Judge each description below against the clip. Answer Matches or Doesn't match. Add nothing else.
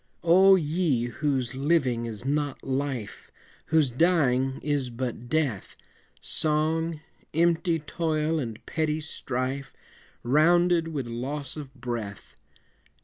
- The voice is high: Doesn't match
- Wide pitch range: Doesn't match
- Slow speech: Matches